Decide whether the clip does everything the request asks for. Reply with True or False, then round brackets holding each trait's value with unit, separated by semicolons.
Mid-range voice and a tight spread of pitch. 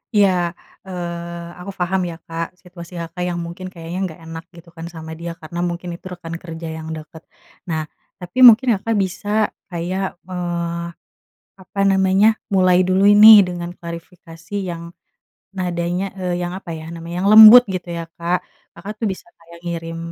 True (175 Hz; 1.8 semitones)